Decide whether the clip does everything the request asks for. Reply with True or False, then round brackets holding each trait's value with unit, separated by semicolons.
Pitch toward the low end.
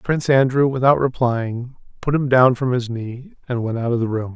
True (125 Hz)